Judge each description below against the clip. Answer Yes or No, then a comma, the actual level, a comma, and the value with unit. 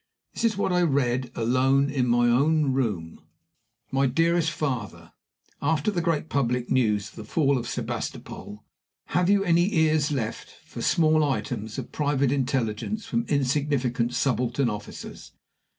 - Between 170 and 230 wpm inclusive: No, average, 145 wpm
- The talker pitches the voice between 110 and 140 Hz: Yes, low, 135 Hz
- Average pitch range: Yes, average, 4.5 semitones